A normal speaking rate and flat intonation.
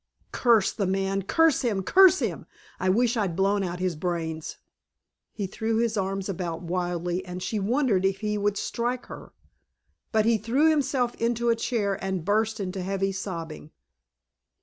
No: average, 165 wpm; average, 3.8 semitones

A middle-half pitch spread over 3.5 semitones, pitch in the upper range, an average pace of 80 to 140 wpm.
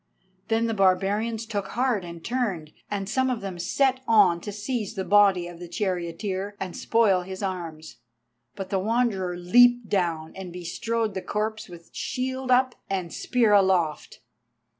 No: average, 4.2 semitones; high, 200 Hz; average, 160 wpm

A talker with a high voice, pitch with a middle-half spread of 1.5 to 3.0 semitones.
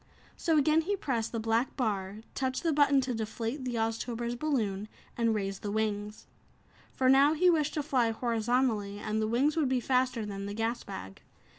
No: high, 235 Hz; average, 3.9 semitones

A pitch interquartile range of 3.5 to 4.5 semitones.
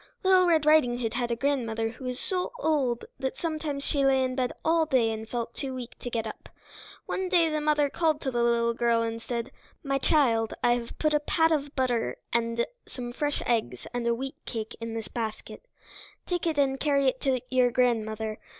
Yes: average, 4.1 semitones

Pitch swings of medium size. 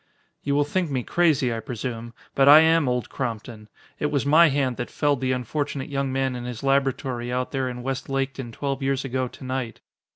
No: narrow, 2.3 semitones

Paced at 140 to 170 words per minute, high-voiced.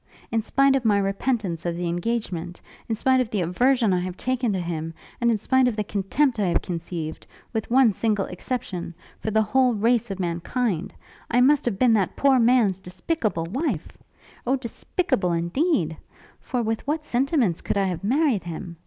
No: average, 185 wpm; high, 215 Hz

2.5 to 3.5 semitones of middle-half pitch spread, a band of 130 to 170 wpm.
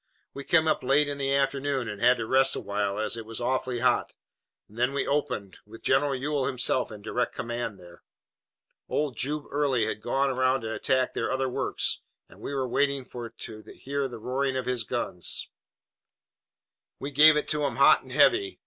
No: average, 2.9 semitones; average, 190 wpm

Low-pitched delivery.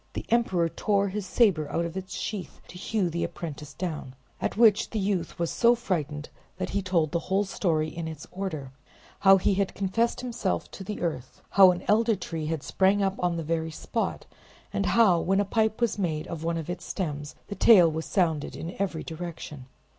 No: medium, 180 Hz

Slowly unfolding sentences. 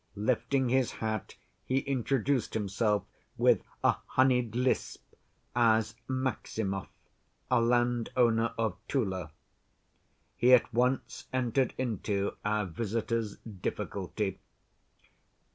Yes: slow, 95 wpm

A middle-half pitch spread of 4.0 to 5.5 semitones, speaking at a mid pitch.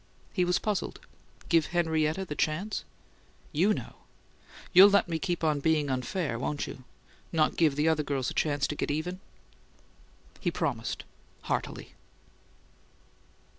No: average, 3.3 semitones; medium, 160 Hz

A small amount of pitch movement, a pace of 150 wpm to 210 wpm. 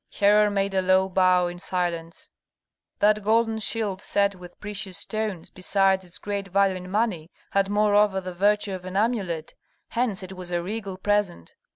Yes: narrow, 2.2 semitones; average, 170 wpm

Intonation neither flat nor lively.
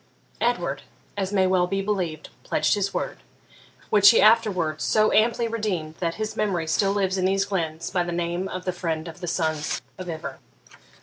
Yes: average, 3.1 semitones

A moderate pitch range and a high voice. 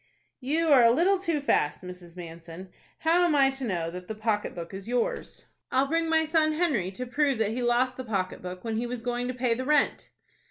No: wide, 7.5 semitones; high, 245 Hz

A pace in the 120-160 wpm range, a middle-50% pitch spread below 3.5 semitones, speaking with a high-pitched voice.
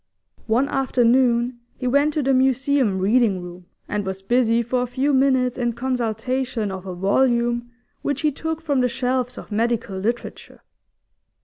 Yes: average, 155 wpm; average, 2.9 semitones; high, 245 Hz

